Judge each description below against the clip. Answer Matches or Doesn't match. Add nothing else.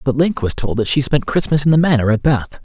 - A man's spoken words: Matches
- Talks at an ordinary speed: Doesn't match